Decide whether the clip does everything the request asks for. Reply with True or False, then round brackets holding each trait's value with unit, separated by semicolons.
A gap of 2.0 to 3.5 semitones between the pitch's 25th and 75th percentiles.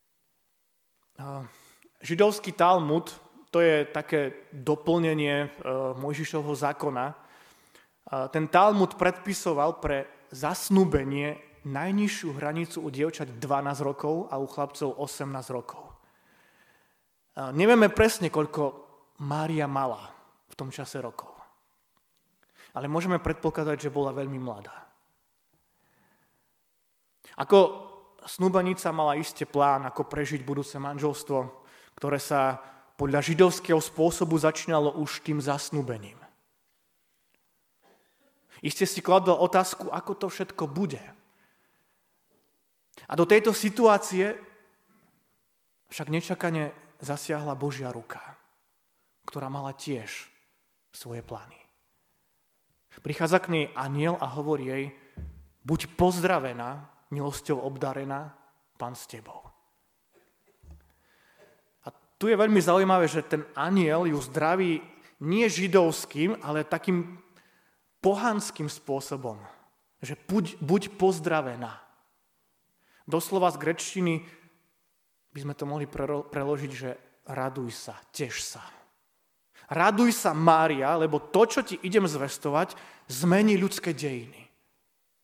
False (4.4 semitones)